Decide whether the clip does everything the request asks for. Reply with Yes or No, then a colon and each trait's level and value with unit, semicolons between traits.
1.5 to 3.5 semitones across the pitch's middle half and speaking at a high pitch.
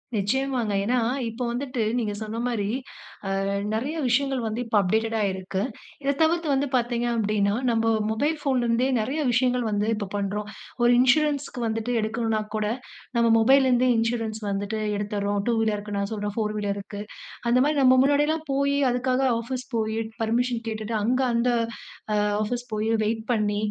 Yes: average, 3.1 semitones; high, 230 Hz